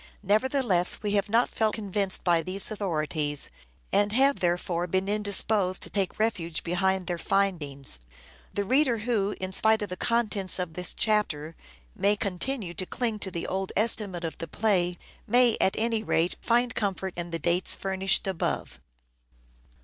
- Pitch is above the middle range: Yes, high, 195 Hz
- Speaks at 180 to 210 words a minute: No, average, 160 wpm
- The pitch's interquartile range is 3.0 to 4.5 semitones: Yes, average, 3.5 semitones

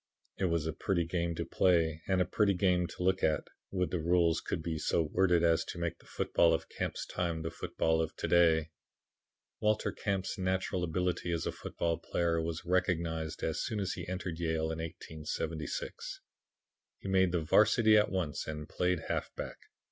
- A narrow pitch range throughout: Yes, narrow, 2.2 semitones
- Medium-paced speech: Yes, average, 185 wpm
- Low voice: Yes, very low, 85 Hz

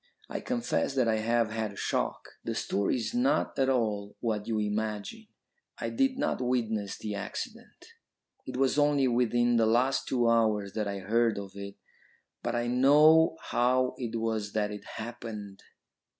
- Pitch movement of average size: Yes, average, 3.4 semitones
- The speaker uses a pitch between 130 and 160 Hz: No, low, 115 Hz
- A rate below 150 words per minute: No, average, 165 wpm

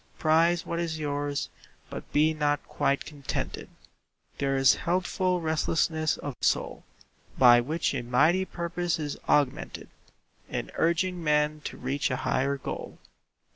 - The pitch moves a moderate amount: Yes, average, 3.1 semitones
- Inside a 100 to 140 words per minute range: Yes, slow, 135 wpm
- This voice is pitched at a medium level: Yes, medium, 155 Hz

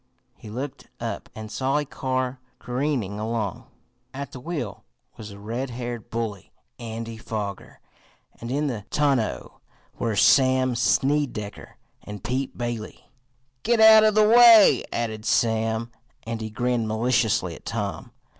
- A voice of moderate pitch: No, low, 120 Hz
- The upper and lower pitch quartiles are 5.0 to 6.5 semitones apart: No, average, 3.5 semitones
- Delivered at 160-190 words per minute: No, slow, 135 wpm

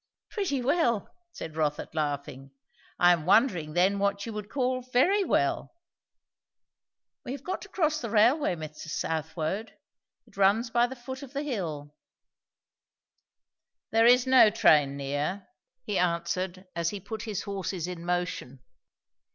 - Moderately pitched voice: No, high, 200 Hz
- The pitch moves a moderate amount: No, wide, 7.0 semitones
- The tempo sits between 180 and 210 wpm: No, average, 145 wpm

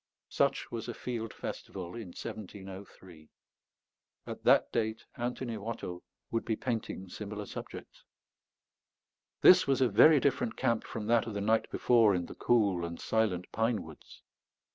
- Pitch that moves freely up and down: No, average, 3.5 semitones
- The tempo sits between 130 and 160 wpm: Yes, average, 145 wpm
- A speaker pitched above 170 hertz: No, low, 110 Hz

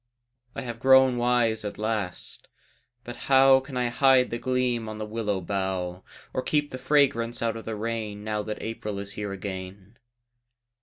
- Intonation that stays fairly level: No, average, 3.5 semitones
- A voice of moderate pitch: No, low, 115 Hz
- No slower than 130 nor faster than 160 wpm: No, average, 170 wpm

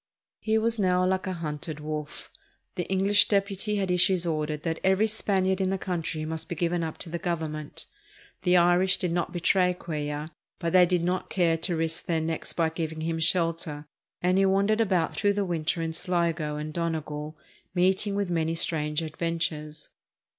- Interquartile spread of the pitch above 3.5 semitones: No, average, 2.8 semitones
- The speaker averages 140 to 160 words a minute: No, average, 180 wpm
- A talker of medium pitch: Yes, medium, 170 Hz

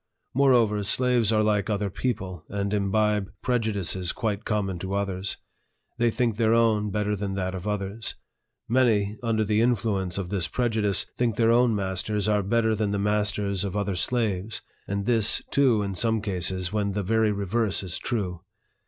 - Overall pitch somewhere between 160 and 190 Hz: No, low, 105 Hz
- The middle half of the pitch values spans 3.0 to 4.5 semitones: No, narrow, 2.4 semitones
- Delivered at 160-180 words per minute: Yes, average, 170 wpm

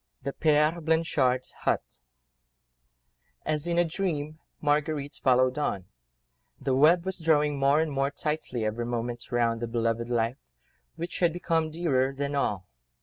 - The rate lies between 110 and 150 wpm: Yes, average, 145 wpm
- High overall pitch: No, medium, 145 Hz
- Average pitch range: Yes, average, 4.5 semitones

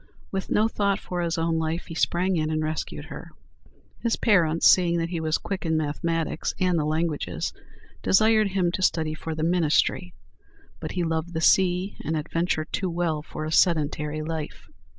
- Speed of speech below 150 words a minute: No, average, 180 wpm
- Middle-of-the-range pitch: Yes, medium, 165 Hz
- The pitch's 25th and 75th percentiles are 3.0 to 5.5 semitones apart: No, narrow, 2.5 semitones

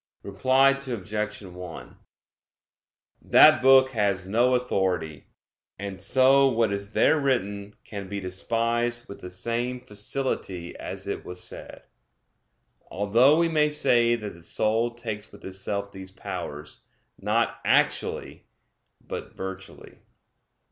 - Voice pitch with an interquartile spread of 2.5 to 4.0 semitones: No, average, 4.5 semitones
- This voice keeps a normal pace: No, slow, 120 wpm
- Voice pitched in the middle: No, low, 105 Hz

